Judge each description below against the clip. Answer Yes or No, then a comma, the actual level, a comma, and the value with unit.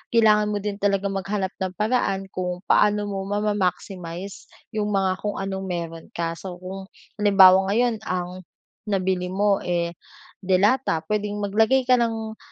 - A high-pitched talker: Yes, high, 195 Hz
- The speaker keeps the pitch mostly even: Yes, narrow, 2.2 semitones